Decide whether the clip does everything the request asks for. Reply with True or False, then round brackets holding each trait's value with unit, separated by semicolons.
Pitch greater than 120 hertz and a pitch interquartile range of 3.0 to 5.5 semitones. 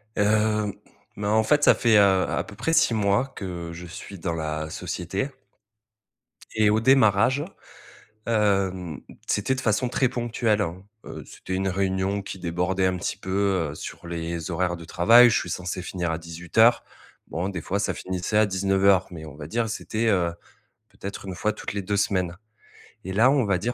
False (95 Hz; 3.6 semitones)